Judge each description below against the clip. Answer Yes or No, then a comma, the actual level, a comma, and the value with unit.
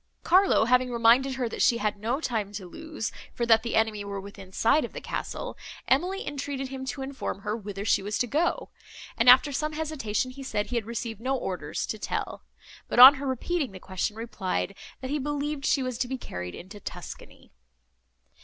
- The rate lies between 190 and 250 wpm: Yes, average, 200 wpm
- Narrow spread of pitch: No, average, 4.6 semitones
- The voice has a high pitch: Yes, high, 245 Hz